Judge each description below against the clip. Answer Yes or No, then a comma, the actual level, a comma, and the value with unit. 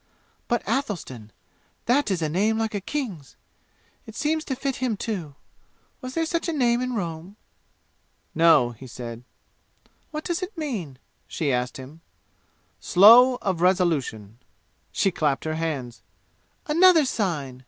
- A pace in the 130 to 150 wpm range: Yes, average, 140 wpm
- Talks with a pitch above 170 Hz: Yes, high, 190 Hz